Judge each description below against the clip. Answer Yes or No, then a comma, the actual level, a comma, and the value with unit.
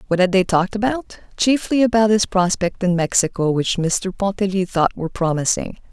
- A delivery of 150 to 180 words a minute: Yes, average, 170 wpm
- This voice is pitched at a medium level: No, high, 195 Hz